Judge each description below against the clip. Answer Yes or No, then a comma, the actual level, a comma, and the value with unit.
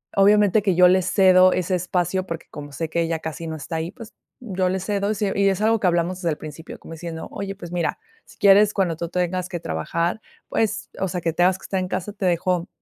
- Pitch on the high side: No, medium, 180 Hz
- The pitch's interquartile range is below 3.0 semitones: Yes, narrow, 2.6 semitones